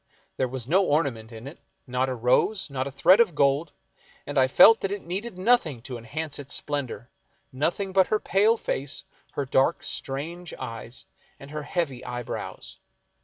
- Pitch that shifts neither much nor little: No, wide, 5.7 semitones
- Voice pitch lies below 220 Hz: Yes, medium, 140 Hz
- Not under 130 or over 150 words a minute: No, average, 175 wpm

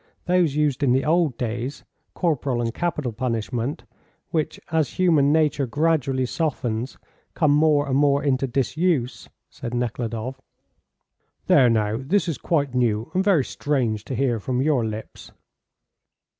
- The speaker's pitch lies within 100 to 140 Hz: Yes, low, 135 Hz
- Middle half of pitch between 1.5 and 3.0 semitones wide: No, average, 4.1 semitones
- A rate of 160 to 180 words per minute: No, average, 140 wpm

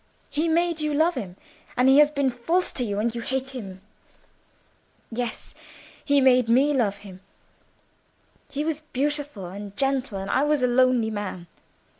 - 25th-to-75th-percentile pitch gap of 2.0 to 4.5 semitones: No, average, 5.2 semitones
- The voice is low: No, very high, 255 Hz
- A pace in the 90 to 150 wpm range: No, average, 165 wpm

